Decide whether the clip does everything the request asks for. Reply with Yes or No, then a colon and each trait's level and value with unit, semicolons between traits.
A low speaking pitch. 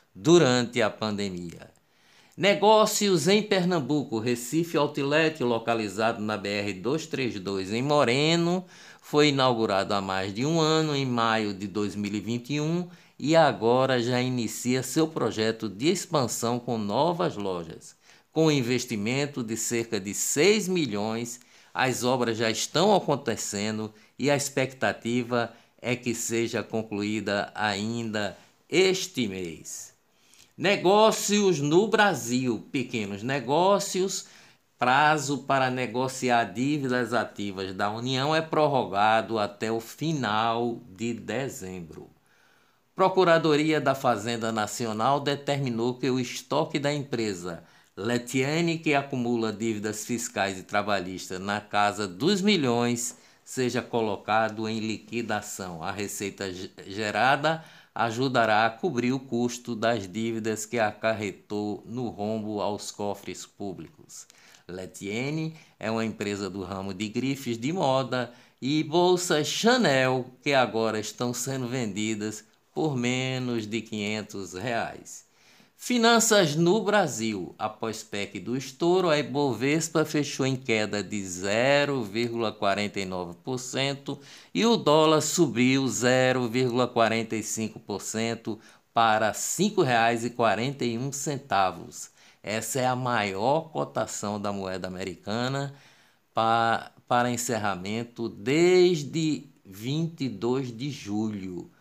Yes: low, 120 Hz